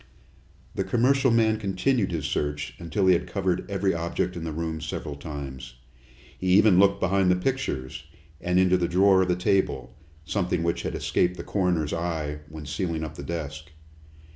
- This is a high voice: No, very low, 90 Hz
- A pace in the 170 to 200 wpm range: Yes, average, 175 wpm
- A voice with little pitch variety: No, average, 3.7 semitones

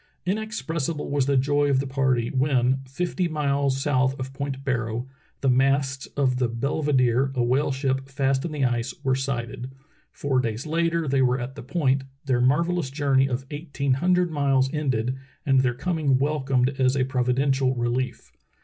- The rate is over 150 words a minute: Yes, average, 170 wpm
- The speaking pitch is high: No, low, 135 Hz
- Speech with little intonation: Yes, narrow, 2.0 semitones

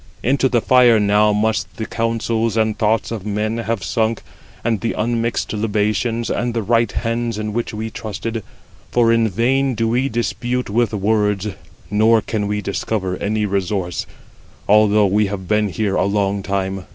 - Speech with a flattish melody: Yes, narrow, 1.9 semitones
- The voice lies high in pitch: No, low, 110 Hz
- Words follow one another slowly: No, average, 170 wpm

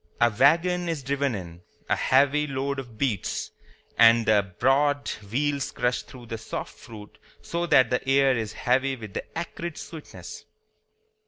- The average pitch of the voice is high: No, low, 135 Hz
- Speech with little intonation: No, average, 4.0 semitones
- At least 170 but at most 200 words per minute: No, average, 155 wpm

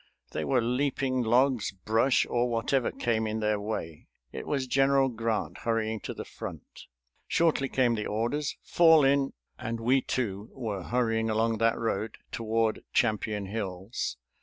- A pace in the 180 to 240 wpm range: No, average, 150 wpm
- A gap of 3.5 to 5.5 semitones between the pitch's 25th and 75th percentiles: No, average, 3.0 semitones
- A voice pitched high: No, low, 115 Hz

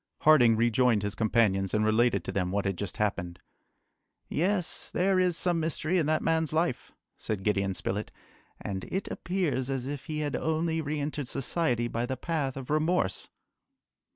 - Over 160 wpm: Yes, average, 170 wpm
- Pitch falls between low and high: No, low, 130 Hz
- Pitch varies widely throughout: Yes, wide, 7.0 semitones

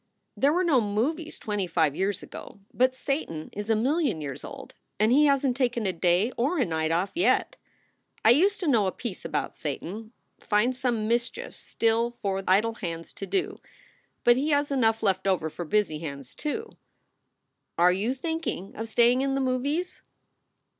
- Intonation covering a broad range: Yes, wide, 6.2 semitones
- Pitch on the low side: No, high, 225 Hz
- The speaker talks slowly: No, average, 180 wpm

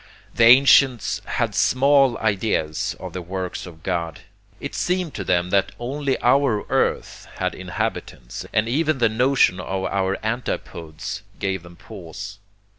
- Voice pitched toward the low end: Yes, low, 105 Hz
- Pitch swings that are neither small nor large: No, wide, 6.1 semitones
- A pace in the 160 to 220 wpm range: No, average, 140 wpm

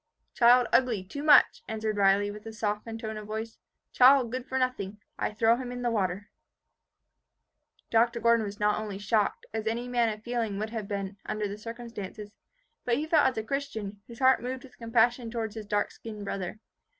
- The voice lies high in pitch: Yes, high, 225 Hz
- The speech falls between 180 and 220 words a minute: Yes, average, 195 wpm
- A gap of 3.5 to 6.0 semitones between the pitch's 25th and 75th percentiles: No, average, 2.7 semitones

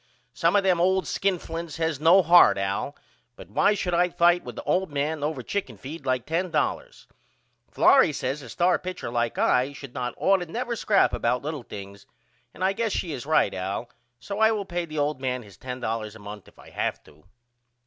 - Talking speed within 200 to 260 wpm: Yes, fast, 205 wpm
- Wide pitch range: Yes, wide, 6.7 semitones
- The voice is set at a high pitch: No, medium, 155 Hz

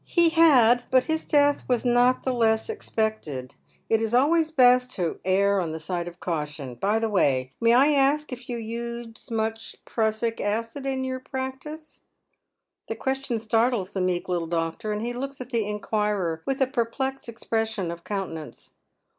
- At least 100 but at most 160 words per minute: No, average, 180 wpm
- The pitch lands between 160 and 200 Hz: No, high, 230 Hz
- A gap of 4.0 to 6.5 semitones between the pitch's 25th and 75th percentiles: Yes, average, 4.9 semitones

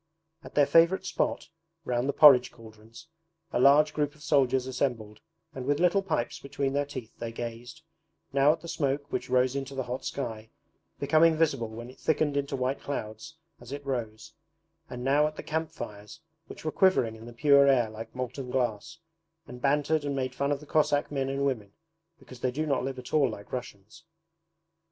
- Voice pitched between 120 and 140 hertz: Yes, low, 135 Hz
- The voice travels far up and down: No, average, 3.3 semitones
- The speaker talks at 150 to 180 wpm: No, average, 195 wpm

